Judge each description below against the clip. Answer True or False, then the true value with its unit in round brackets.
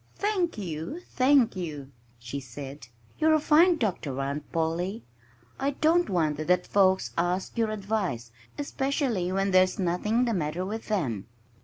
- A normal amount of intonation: False (8.0 semitones)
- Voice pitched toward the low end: False (185 Hz)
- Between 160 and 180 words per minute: False (145 wpm)